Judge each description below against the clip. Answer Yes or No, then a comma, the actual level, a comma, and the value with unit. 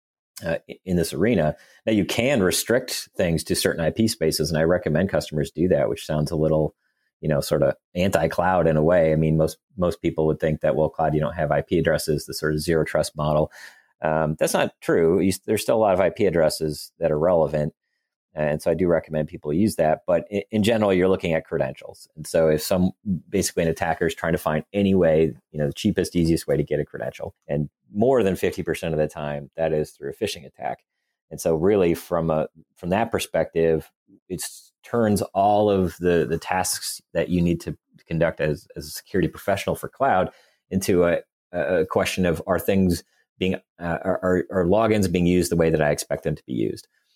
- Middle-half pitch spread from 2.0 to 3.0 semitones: Yes, average, 2.7 semitones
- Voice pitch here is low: Yes, very low, 80 Hz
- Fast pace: Yes, fast, 215 wpm